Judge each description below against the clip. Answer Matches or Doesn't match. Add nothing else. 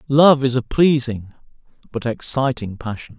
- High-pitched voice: Doesn't match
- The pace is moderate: Doesn't match